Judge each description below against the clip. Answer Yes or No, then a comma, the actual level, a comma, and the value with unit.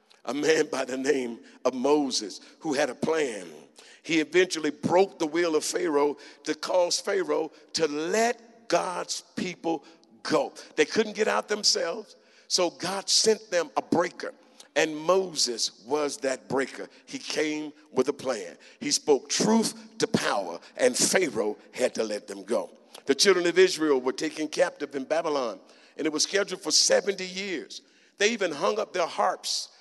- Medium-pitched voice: Yes, medium, 175 Hz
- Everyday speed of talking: Yes, average, 165 wpm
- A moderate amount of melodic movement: No, wide, 5.7 semitones